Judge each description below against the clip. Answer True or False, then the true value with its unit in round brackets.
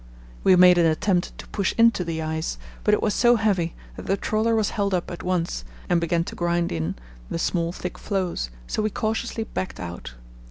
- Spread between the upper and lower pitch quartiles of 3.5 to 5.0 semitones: True (3.9 semitones)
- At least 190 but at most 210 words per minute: True (205 wpm)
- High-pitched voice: False (180 Hz)